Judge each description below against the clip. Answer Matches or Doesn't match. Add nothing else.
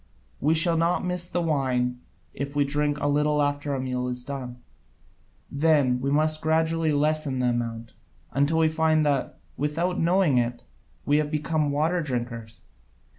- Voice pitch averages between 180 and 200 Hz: Doesn't match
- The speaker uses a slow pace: Doesn't match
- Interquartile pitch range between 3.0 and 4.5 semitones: Matches